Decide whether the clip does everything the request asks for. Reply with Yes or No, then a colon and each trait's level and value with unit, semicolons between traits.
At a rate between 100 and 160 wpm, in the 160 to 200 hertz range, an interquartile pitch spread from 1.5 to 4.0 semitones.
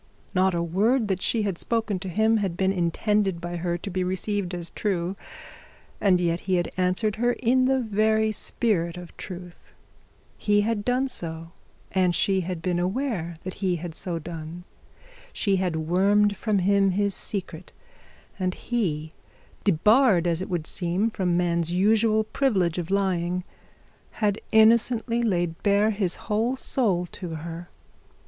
Yes: average, 155 wpm; high, 190 Hz; average, 3.7 semitones